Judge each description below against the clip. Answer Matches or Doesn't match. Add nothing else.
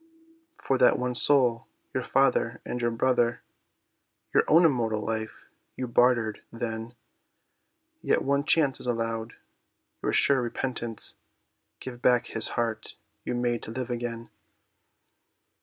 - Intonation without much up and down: Matches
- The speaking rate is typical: Doesn't match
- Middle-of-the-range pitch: Doesn't match